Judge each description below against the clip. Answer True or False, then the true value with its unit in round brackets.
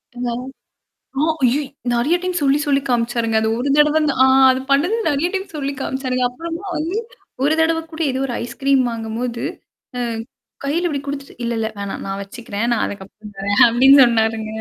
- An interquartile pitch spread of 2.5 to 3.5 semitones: False (4.1 semitones)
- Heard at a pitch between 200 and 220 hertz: False (255 Hz)